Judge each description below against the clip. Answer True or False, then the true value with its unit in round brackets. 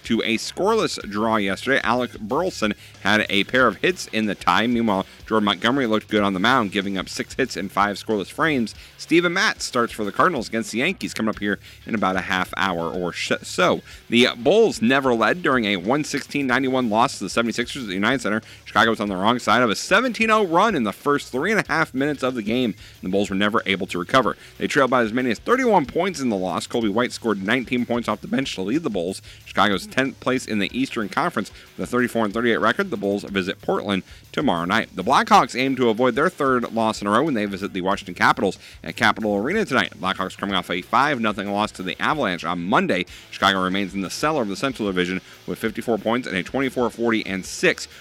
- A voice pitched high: False (105 Hz)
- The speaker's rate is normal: False (225 wpm)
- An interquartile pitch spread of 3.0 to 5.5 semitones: True (4.1 semitones)